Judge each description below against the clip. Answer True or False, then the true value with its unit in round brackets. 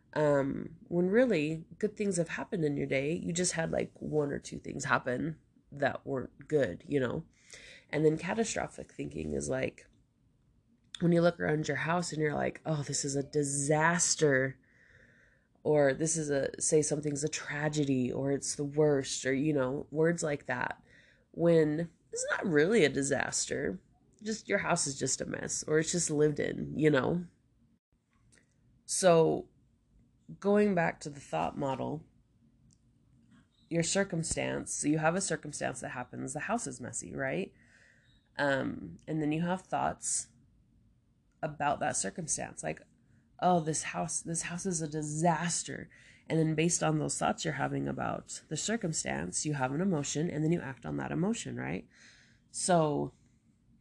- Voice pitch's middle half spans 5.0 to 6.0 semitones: False (3.9 semitones)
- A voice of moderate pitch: True (150 Hz)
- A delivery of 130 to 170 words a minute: True (160 wpm)